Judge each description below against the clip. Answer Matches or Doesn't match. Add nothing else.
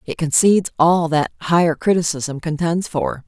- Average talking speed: Matches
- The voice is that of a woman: Matches